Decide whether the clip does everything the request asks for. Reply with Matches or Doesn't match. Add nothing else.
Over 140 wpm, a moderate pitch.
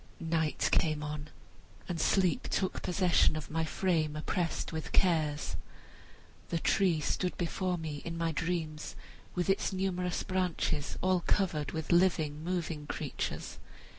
Doesn't match